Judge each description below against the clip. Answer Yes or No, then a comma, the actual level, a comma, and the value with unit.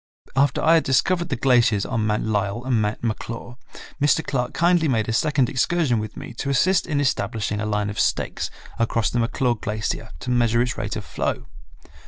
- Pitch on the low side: Yes, low, 120 Hz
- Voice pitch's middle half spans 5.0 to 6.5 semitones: No, average, 3.9 semitones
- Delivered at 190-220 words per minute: Yes, average, 195 wpm